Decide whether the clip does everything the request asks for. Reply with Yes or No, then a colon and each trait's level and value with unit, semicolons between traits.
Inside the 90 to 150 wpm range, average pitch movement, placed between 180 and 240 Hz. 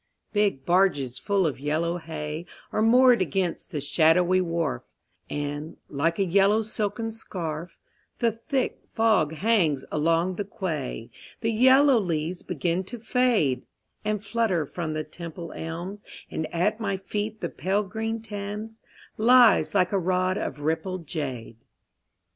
Yes: average, 140 wpm; average, 5.0 semitones; medium, 185 Hz